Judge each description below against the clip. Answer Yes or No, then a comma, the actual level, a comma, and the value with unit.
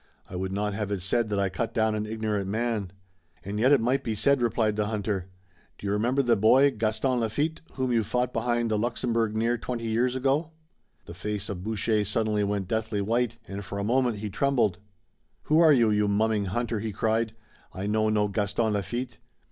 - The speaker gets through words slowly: No, fast, 205 wpm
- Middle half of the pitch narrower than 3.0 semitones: Yes, narrow, 2.5 semitones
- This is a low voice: Yes, low, 110 Hz